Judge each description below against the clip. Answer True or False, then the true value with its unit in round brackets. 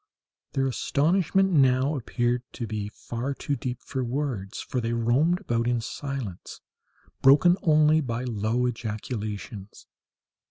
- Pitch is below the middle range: True (125 Hz)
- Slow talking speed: True (125 wpm)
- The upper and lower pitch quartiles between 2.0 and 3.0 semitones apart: False (3.6 semitones)